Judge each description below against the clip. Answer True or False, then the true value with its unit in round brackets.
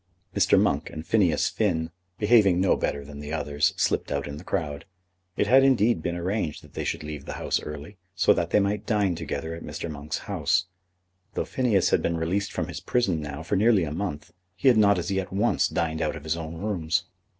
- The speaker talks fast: True (215 wpm)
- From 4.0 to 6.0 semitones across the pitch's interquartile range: True (4.6 semitones)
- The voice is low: True (85 Hz)